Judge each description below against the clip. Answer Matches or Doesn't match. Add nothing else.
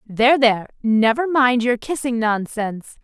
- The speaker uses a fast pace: Doesn't match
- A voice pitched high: Matches